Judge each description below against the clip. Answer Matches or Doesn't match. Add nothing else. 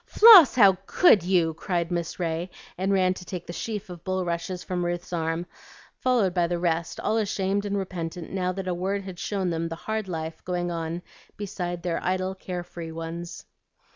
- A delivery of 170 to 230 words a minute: Matches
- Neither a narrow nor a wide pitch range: Doesn't match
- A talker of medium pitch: Matches